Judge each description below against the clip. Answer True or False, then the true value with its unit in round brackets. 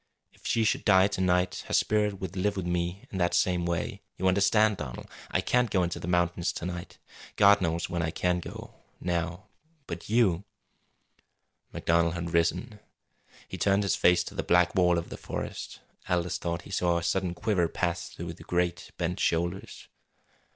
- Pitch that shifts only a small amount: True (2.0 semitones)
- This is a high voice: False (90 Hz)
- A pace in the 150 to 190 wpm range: True (185 wpm)